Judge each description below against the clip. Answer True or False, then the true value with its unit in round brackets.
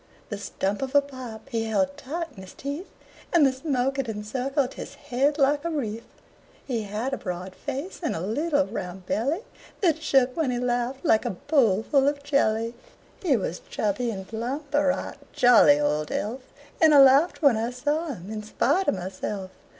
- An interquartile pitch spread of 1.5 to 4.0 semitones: False (4.9 semitones)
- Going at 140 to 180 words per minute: False (190 wpm)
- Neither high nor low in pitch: False (255 Hz)